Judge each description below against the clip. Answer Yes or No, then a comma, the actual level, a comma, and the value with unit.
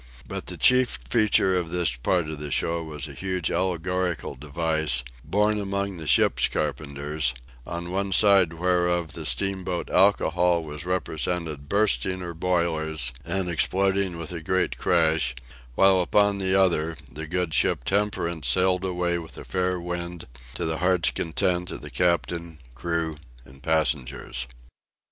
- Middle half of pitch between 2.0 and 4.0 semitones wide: Yes, average, 2.8 semitones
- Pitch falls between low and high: No, very low, 85 Hz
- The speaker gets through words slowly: No, average, 150 wpm